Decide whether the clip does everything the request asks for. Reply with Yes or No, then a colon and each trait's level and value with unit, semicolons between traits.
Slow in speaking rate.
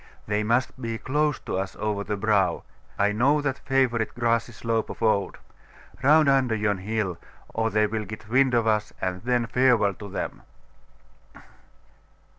No: average, 160 wpm